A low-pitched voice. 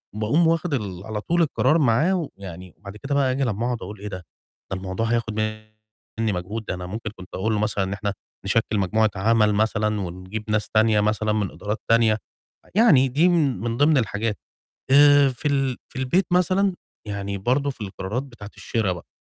Yes: low, 110 Hz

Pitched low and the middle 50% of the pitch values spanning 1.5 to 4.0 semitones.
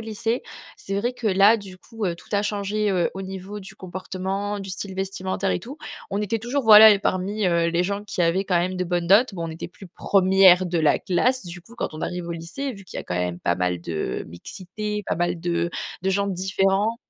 No: high, 190 Hz; average, 2.9 semitones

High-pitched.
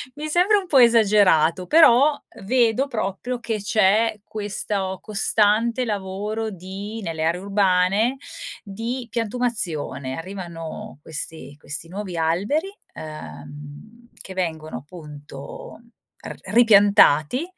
Yes: high, 200 Hz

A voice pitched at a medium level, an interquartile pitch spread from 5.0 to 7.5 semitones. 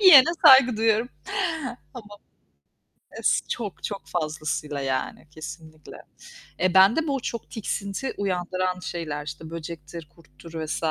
Yes: medium, 175 Hz; wide, 5.6 semitones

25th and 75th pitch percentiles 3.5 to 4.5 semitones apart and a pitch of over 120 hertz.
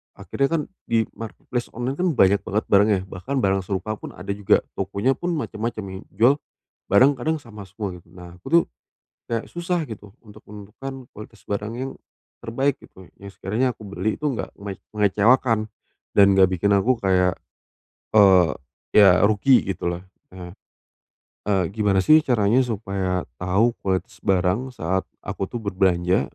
No: average, 4.1 semitones; low, 105 Hz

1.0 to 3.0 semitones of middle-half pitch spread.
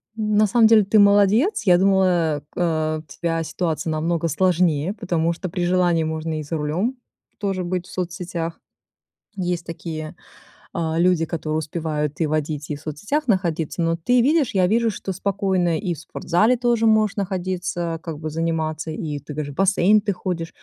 No: average, 3.6 semitones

